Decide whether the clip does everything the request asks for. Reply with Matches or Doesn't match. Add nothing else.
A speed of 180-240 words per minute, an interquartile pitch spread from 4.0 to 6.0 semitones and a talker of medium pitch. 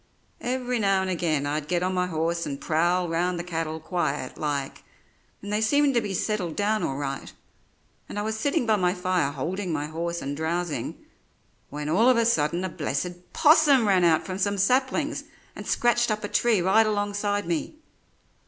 Matches